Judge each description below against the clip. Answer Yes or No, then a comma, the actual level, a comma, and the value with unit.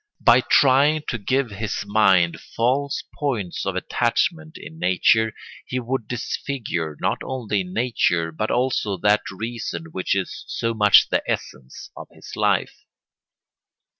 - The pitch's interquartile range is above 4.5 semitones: Yes, average, 5.0 semitones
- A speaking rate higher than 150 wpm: No, slow, 135 wpm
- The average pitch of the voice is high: No, low, 110 Hz